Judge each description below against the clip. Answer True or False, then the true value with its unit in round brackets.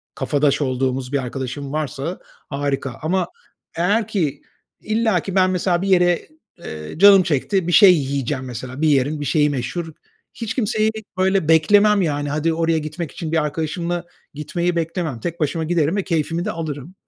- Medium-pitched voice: True (160 Hz)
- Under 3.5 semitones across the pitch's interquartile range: False (4.0 semitones)